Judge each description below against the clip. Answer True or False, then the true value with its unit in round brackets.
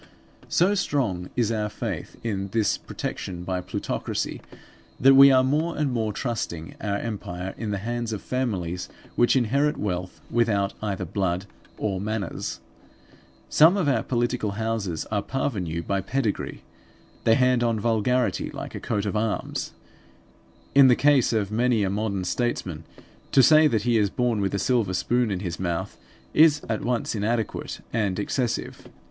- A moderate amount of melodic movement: True (4.1 semitones)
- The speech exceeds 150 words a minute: True (160 wpm)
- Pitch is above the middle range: False (110 Hz)